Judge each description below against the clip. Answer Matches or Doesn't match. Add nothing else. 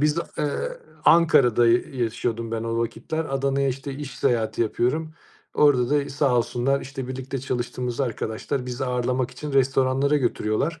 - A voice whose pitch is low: Matches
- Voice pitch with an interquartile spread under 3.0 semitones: Matches